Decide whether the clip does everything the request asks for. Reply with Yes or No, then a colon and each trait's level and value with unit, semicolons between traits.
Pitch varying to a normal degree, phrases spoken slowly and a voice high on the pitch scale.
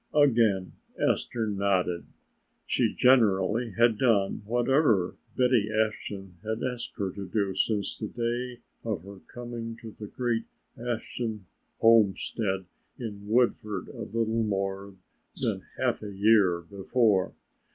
No: average, 3.1 semitones; slow, 120 wpm; low, 110 Hz